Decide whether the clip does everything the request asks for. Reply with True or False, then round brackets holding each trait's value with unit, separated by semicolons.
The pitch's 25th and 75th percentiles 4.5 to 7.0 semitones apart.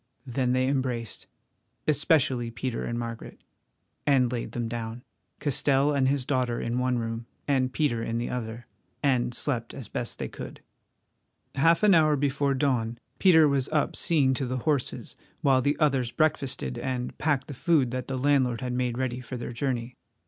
False (2.8 semitones)